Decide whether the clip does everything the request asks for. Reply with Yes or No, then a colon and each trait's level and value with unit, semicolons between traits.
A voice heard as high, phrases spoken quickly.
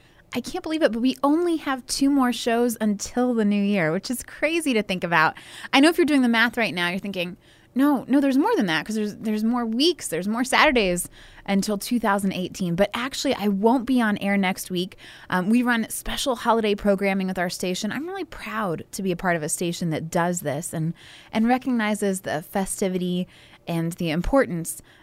Yes: high, 210 Hz; fast, 210 wpm